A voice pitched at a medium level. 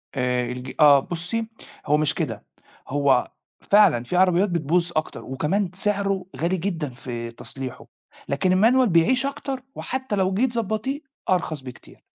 Yes: medium, 175 Hz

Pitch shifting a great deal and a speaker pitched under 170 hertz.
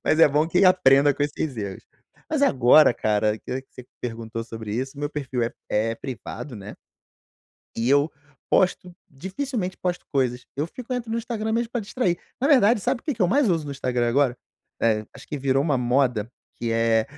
Yes: wide, 7.6 semitones; medium, 140 Hz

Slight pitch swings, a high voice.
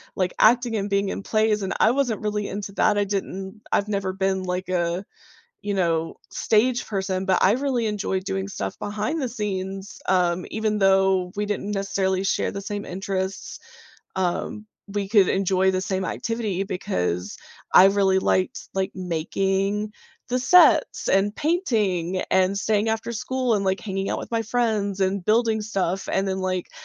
Yes: narrow, 2.1 semitones; high, 195 Hz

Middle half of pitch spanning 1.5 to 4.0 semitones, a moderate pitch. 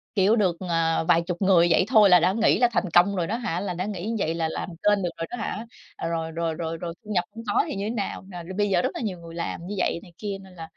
Yes: average, 3.3 semitones; medium, 180 Hz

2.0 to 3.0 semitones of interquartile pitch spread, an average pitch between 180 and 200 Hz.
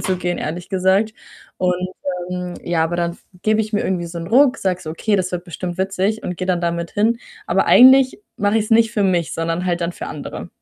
No: average, 3.6 semitones; medium, 185 Hz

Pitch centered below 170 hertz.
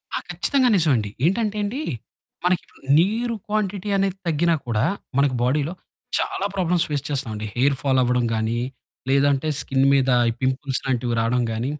Yes: medium, 140 Hz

